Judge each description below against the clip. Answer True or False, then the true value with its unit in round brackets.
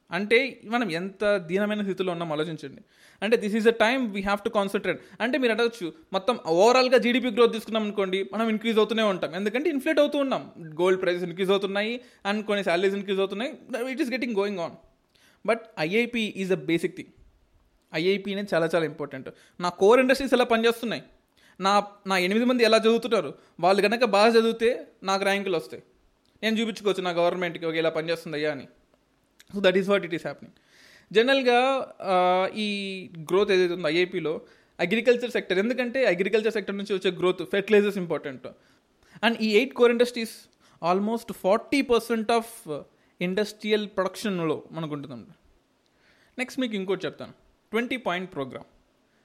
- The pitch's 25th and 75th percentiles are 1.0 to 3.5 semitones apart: False (4.2 semitones)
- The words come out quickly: True (155 wpm)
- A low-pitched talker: False (205 Hz)